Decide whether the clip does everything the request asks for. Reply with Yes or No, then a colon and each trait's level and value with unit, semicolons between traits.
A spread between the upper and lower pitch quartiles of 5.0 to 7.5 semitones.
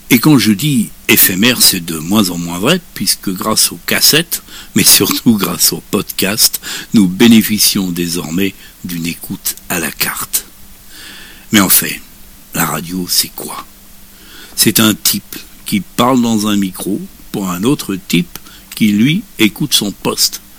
Yes: average, 5.3 semitones